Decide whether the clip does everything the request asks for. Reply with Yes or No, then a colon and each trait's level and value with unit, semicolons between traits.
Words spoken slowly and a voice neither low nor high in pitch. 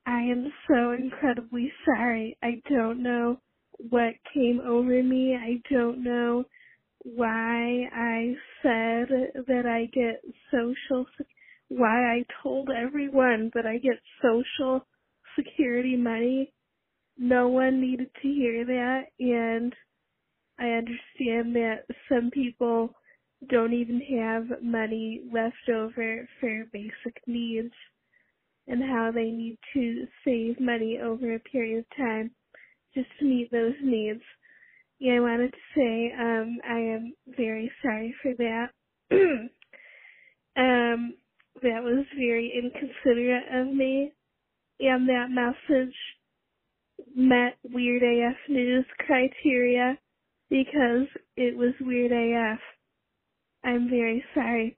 No: slow, 115 wpm; high, 245 Hz